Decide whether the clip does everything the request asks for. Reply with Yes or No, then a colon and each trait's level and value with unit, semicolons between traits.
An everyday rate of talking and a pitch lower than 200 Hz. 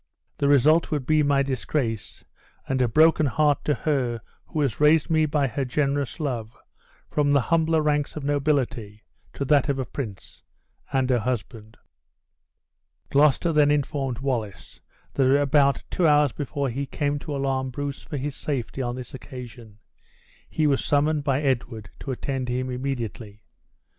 Yes: average, 160 wpm; medium, 140 Hz